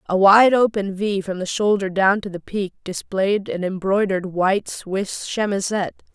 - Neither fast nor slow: Yes, average, 165 wpm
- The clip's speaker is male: No, female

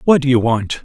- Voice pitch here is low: Yes, low, 130 Hz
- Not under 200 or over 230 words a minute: No, fast, 285 wpm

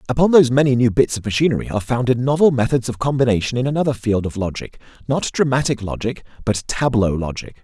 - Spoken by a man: Yes, male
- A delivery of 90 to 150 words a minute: No, average, 190 wpm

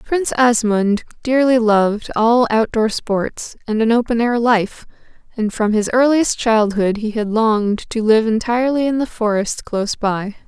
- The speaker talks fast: No, average, 160 wpm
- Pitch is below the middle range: No, high, 225 Hz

